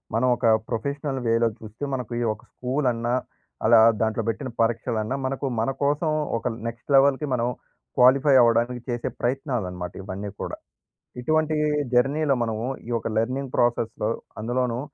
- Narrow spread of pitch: No, average, 3.0 semitones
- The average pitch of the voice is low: Yes, low, 120 Hz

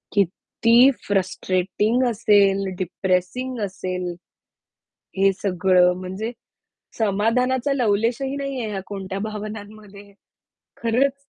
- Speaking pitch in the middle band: No, high, 205 Hz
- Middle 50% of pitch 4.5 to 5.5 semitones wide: No, average, 3.7 semitones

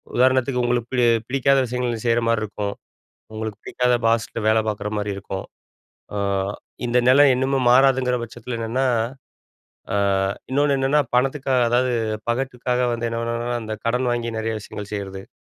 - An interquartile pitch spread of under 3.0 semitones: Yes, narrow, 2.5 semitones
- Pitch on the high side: No, low, 120 Hz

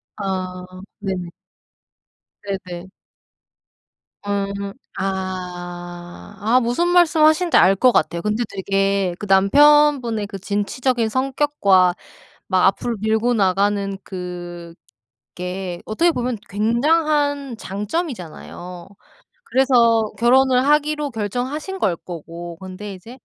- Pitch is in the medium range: No, high, 205 Hz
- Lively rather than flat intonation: Yes, wide, 5.8 semitones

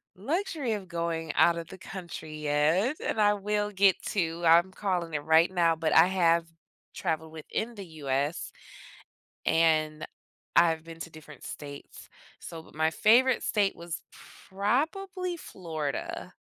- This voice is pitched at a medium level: Yes, medium, 170 Hz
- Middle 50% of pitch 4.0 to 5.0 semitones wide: Yes, average, 4.4 semitones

